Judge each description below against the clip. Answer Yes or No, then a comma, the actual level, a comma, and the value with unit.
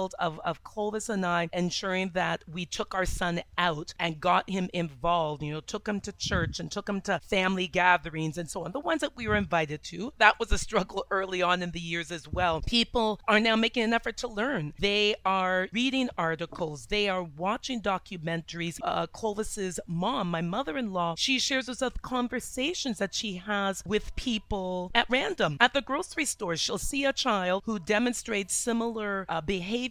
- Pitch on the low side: No, high, 200 Hz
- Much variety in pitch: No, average, 4.5 semitones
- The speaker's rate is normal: Yes, average, 195 wpm